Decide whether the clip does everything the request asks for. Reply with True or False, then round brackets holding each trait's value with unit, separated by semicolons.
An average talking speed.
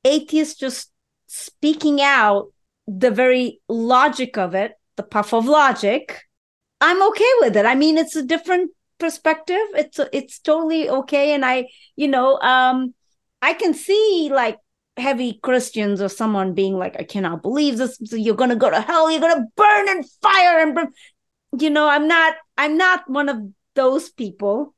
True (175 wpm)